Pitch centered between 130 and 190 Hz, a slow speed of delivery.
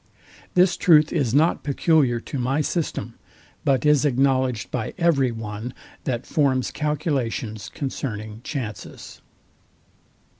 Yes: low, 135 Hz; slow, 110 wpm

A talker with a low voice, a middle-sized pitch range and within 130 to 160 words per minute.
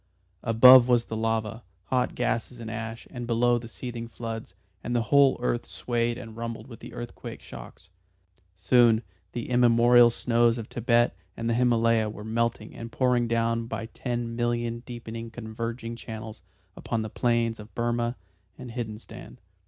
No: low, 115 Hz; narrow, 1.0 semitones; average, 155 wpm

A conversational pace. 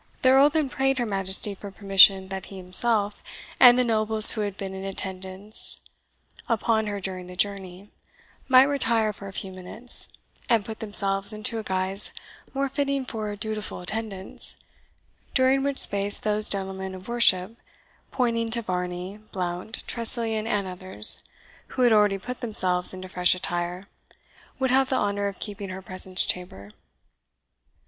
Yes: average, 155 wpm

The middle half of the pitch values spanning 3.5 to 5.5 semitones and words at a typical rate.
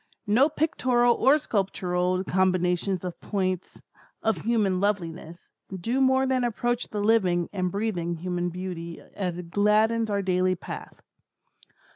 No: average, 4.1 semitones; slow, 130 wpm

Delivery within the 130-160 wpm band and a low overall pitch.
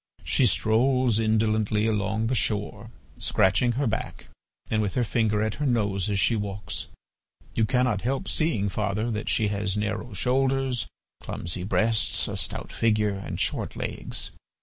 Yes: average, 150 wpm; low, 110 Hz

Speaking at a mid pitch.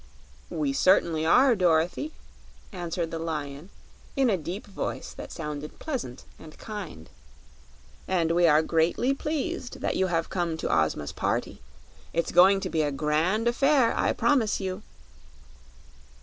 Yes: medium, 175 Hz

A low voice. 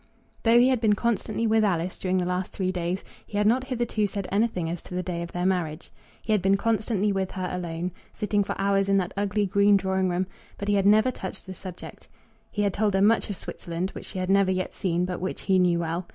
No: high, 195 Hz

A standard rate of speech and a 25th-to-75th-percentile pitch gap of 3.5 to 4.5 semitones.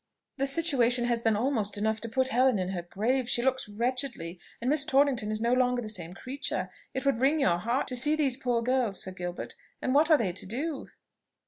No: fast, 220 wpm; average, 3.8 semitones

